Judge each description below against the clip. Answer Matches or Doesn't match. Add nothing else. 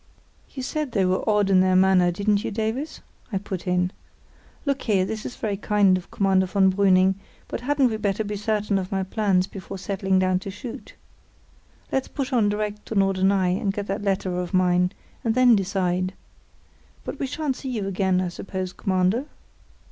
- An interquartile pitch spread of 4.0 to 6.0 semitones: Doesn't match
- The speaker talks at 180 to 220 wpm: Matches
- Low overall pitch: Doesn't match